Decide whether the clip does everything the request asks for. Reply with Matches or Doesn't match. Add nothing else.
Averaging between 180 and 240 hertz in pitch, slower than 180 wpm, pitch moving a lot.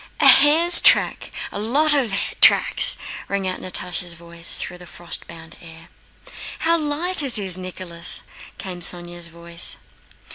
Matches